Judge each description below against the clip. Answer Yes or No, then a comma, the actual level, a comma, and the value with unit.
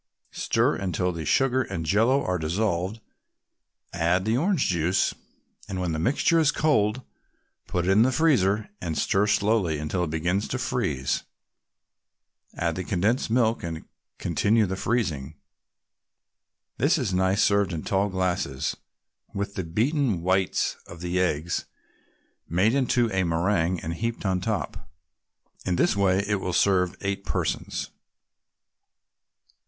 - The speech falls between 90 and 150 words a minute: Yes, average, 140 wpm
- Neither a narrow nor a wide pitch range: Yes, average, 4.1 semitones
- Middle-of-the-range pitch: No, very low, 95 Hz